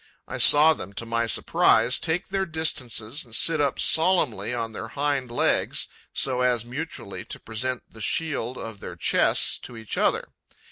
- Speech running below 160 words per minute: No, average, 170 wpm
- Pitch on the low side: Yes, low, 125 Hz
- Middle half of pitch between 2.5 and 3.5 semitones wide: No, average, 4.9 semitones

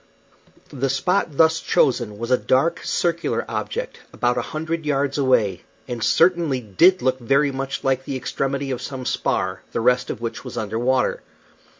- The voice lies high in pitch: No, low, 135 Hz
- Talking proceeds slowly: No, average, 170 wpm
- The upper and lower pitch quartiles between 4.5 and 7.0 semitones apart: No, average, 3.5 semitones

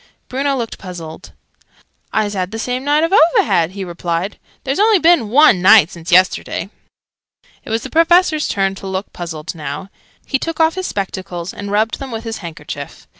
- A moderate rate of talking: Yes, average, 175 wpm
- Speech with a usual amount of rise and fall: No, wide, 7.8 semitones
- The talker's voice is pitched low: No, high, 205 Hz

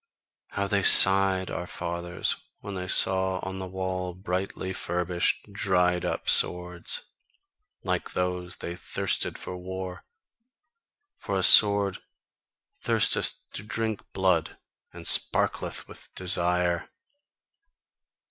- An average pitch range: No, narrow, 1.3 semitones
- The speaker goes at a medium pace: No, slow, 110 wpm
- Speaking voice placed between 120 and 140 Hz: No, very low, 95 Hz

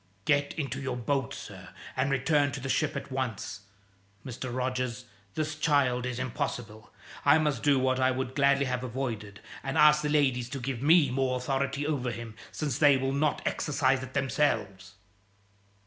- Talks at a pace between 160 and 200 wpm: Yes, average, 170 wpm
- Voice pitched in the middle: No, low, 130 Hz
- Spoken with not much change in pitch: Yes, narrow, 2.3 semitones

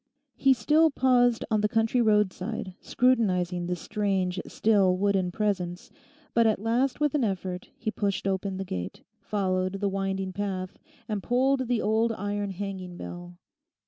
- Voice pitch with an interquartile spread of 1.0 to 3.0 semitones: No, average, 3.5 semitones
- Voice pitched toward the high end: Yes, high, 200 Hz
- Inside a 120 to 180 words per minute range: Yes, average, 150 wpm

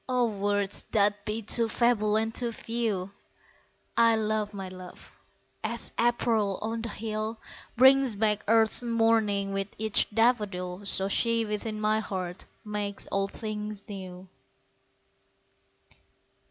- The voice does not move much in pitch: Yes, narrow, 2.1 semitones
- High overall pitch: Yes, high, 215 Hz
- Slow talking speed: Yes, slow, 125 wpm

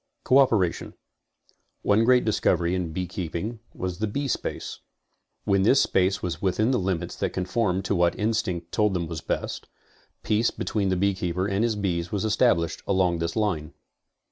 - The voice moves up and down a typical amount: Yes, average, 3.6 semitones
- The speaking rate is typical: Yes, average, 160 wpm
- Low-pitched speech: Yes, very low, 95 Hz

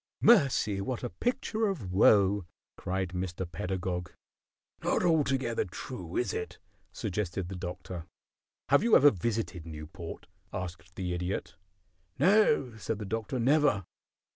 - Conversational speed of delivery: No, slow, 125 wpm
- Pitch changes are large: Yes, wide, 6.5 semitones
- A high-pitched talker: No, low, 100 Hz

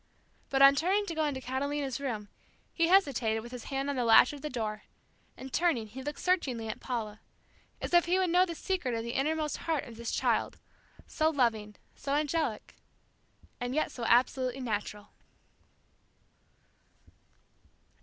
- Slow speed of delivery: No, average, 165 wpm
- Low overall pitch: No, very high, 270 Hz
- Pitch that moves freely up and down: No, average, 4.9 semitones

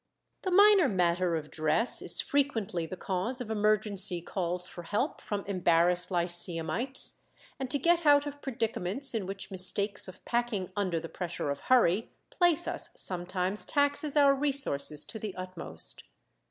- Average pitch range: No, wide, 7.1 semitones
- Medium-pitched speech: No, high, 200 Hz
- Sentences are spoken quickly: No, average, 155 wpm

